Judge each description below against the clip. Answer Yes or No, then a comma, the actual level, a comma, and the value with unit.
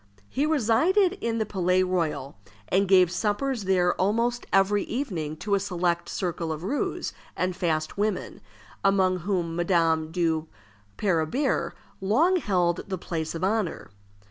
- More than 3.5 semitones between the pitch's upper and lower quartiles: Yes, average, 4.0 semitones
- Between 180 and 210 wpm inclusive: No, average, 140 wpm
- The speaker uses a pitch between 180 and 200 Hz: Yes, medium, 185 Hz